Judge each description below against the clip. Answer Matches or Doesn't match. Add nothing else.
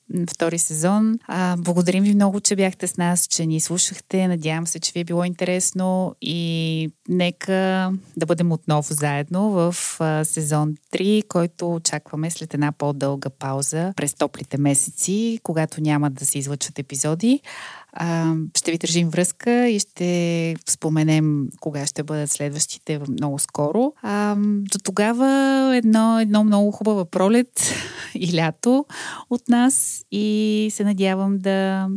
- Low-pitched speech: Doesn't match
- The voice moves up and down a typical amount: Matches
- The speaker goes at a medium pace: Matches